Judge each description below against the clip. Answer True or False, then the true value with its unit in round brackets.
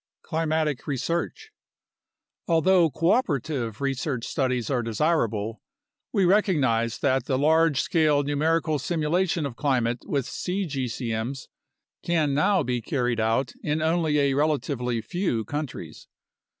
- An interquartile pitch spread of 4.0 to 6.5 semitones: True (4.7 semitones)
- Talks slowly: True (110 wpm)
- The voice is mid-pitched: True (145 Hz)